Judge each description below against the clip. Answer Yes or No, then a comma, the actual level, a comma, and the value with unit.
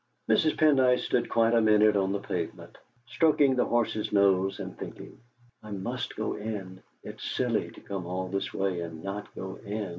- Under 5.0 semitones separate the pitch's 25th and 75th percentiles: Yes, average, 3.3 semitones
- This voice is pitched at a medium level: No, low, 100 Hz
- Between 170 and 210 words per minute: Yes, average, 180 wpm